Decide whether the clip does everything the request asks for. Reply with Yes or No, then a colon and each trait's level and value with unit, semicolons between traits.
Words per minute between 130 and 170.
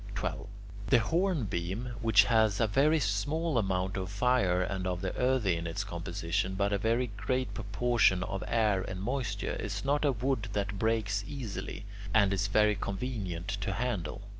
Yes: average, 165 wpm